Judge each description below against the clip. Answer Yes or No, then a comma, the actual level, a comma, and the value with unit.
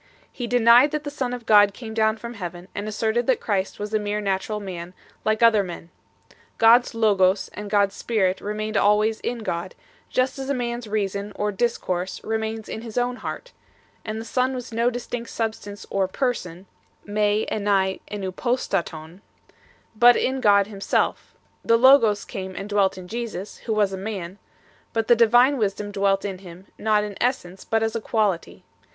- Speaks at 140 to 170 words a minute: No, average, 185 wpm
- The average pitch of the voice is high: Yes, high, 215 Hz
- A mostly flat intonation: No, average, 3.1 semitones